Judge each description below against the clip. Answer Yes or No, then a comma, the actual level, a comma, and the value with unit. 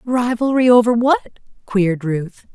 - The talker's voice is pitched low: No, high, 230 Hz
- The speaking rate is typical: No, slow, 120 wpm